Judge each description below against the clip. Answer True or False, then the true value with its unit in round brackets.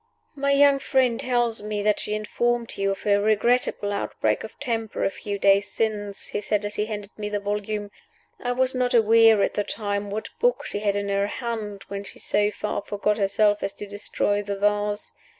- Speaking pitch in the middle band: False (210 Hz)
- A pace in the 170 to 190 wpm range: False (205 wpm)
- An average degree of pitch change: False (2.0 semitones)